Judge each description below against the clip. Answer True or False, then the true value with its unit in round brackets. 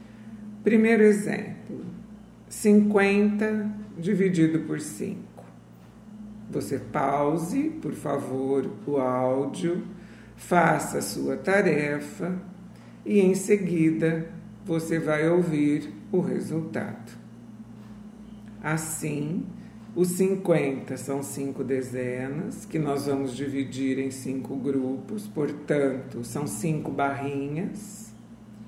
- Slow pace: True (85 wpm)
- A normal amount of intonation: False (6.9 semitones)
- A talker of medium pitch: True (155 Hz)